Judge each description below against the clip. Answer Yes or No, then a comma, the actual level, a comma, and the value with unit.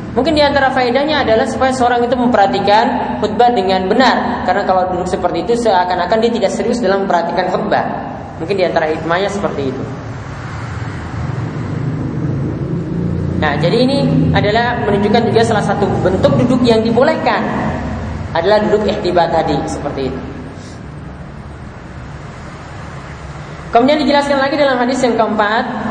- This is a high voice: Yes, high, 205 Hz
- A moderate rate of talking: No, slow, 125 wpm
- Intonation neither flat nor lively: No, wide, 6.3 semitones